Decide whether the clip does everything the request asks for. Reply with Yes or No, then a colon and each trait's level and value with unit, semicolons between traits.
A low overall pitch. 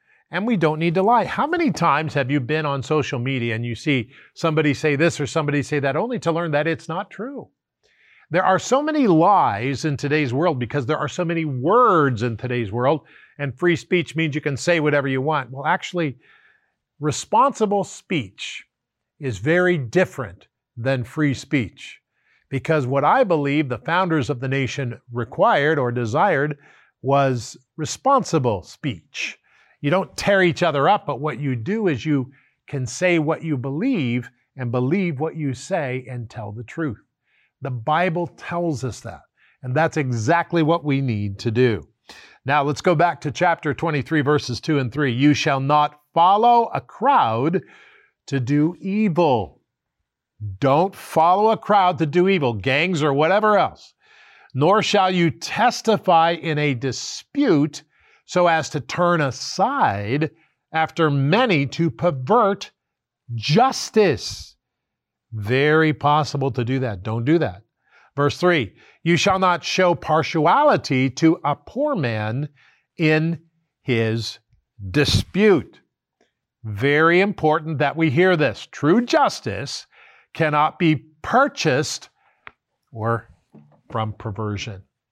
No: medium, 150 Hz